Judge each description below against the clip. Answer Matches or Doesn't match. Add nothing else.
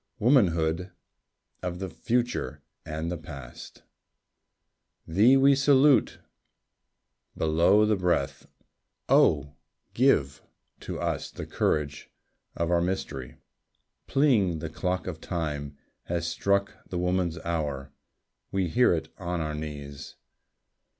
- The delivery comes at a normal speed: Doesn't match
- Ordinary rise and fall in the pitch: Matches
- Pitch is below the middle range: Matches